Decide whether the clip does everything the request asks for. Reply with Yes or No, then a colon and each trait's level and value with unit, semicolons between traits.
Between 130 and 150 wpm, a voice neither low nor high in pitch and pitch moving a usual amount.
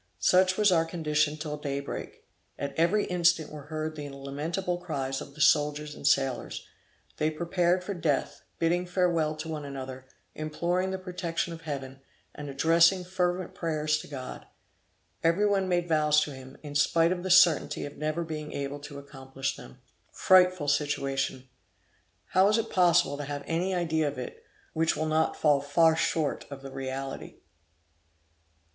No: average, 165 wpm; medium, 155 Hz; average, 3.5 semitones